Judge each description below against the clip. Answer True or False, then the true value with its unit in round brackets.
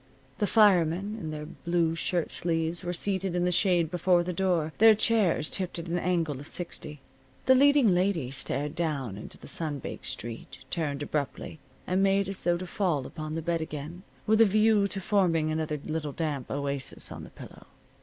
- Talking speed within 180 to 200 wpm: True (190 wpm)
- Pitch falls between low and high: True (170 Hz)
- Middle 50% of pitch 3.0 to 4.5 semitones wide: True (3.6 semitones)